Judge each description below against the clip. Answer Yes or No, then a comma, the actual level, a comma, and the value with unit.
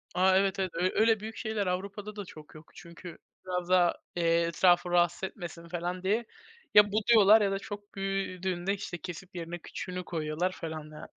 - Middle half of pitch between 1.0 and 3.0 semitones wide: Yes, narrow, 2.5 semitones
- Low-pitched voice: No, medium, 185 Hz